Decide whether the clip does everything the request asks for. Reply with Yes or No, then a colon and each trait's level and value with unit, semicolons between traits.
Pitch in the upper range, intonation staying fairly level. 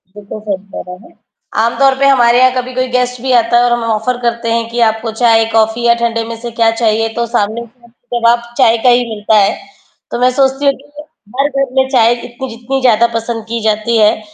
Yes: high, 235 Hz; narrow, 1.9 semitones